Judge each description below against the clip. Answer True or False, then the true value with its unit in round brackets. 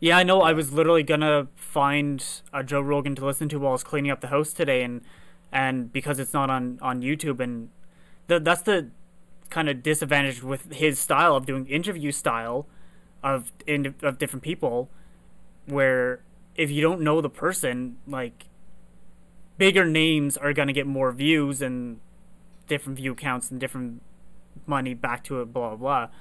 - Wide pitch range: False (3.2 semitones)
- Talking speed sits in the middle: True (175 wpm)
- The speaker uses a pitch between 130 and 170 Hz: True (140 Hz)